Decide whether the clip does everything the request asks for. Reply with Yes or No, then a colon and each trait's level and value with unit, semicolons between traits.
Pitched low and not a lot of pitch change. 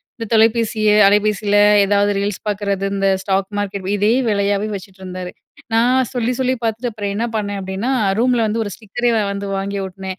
No: high, 205 Hz; narrow, 2.3 semitones